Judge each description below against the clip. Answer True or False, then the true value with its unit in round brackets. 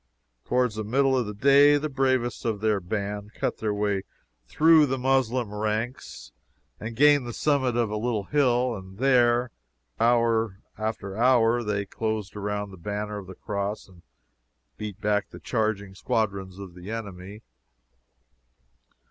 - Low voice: True (110 Hz)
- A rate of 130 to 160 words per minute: True (150 wpm)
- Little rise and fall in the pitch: False (3.3 semitones)